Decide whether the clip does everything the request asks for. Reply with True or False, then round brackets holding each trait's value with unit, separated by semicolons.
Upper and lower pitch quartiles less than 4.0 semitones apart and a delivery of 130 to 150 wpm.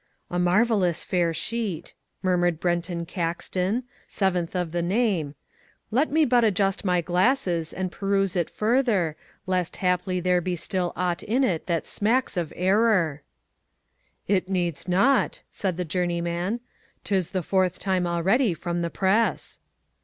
True (2.8 semitones; 140 wpm)